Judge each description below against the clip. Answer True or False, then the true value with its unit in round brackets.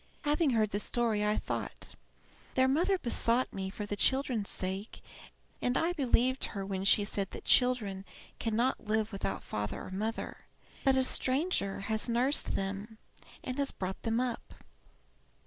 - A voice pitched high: True (225 Hz)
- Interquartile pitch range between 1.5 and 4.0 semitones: False (4.5 semitones)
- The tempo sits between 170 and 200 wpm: False (155 wpm)